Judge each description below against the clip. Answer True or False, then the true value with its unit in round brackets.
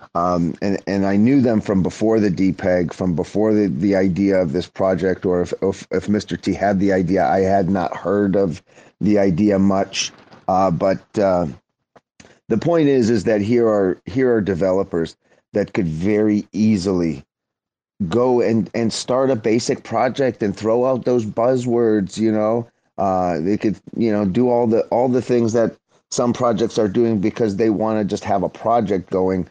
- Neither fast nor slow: True (185 wpm)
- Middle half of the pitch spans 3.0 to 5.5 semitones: True (3.4 semitones)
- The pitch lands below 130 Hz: True (105 Hz)